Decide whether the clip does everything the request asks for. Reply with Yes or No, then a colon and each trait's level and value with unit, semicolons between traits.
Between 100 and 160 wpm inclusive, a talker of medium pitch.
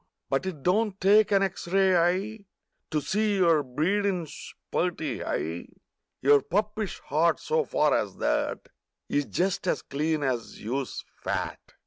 Yes: average, 145 wpm; medium, 175 Hz